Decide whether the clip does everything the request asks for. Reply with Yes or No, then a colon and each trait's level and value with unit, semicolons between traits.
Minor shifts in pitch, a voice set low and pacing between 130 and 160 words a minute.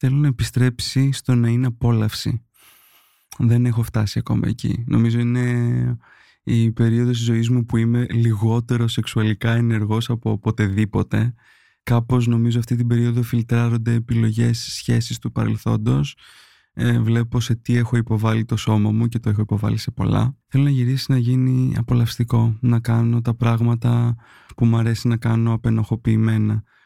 Yes: narrow, 1.2 semitones; low, 120 Hz; average, 145 wpm